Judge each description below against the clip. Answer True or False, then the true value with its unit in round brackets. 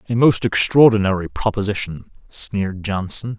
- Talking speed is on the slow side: True (105 wpm)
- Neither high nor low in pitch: False (105 Hz)